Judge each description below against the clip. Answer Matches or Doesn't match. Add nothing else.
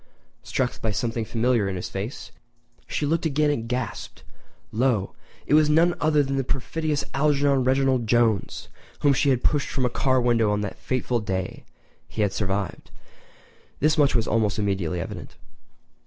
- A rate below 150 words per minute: Doesn't match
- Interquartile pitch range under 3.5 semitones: Doesn't match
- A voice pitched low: Matches